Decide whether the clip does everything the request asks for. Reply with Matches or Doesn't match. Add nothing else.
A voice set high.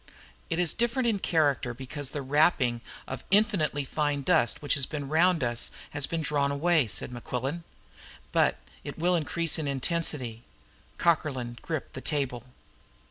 Doesn't match